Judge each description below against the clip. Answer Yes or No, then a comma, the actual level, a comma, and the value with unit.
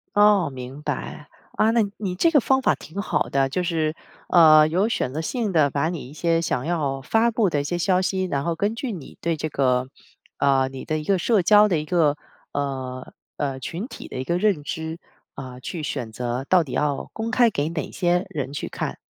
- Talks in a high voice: No, medium, 160 Hz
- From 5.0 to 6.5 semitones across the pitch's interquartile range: Yes, average, 5.3 semitones